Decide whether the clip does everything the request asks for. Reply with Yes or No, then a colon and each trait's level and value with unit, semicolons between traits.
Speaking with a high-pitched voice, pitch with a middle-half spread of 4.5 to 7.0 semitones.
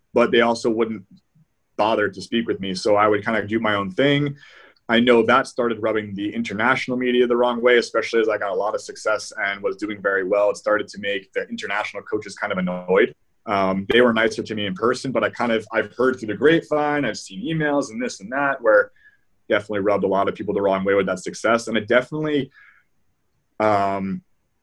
No: low, 115 Hz; average, 5.0 semitones